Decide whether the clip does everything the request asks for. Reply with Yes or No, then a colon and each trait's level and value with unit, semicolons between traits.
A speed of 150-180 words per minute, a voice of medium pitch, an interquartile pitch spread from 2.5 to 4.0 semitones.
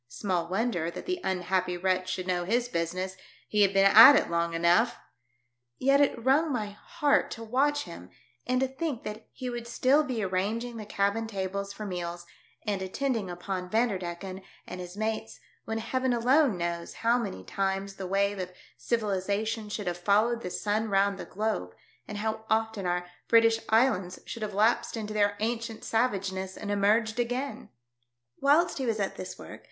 No: average, 175 wpm; high, 210 Hz; average, 3.7 semitones